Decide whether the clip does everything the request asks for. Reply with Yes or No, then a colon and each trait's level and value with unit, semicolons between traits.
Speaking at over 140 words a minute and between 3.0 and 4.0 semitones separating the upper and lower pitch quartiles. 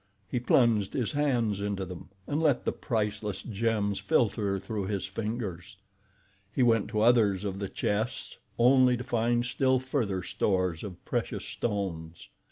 Yes: average, 150 wpm; average, 3.6 semitones